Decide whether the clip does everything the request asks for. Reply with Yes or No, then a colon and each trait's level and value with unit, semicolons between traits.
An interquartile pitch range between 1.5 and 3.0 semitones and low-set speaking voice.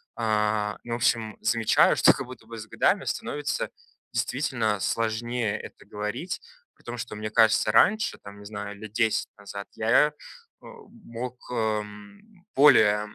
Yes: narrow, 2.4 semitones; low, 110 Hz